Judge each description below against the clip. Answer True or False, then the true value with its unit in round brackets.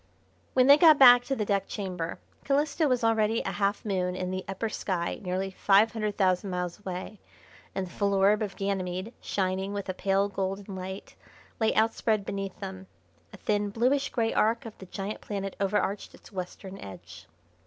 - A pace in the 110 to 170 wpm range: False (180 wpm)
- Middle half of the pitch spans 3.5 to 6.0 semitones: False (2.6 semitones)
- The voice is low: False (200 Hz)